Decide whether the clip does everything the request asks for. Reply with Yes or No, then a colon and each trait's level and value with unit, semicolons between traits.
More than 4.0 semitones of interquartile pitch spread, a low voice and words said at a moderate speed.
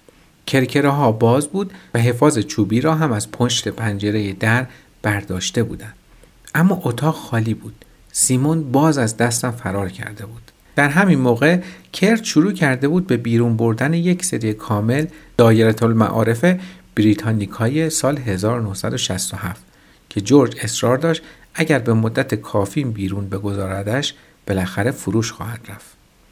Yes: wide, 5.6 semitones; low, 120 Hz; average, 135 wpm